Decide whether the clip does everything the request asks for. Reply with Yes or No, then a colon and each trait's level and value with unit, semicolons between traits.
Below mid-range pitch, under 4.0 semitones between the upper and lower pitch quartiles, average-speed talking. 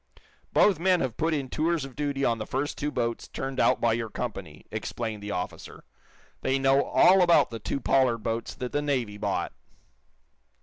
No: low, 130 Hz; average, 4.3 semitones; average, 185 wpm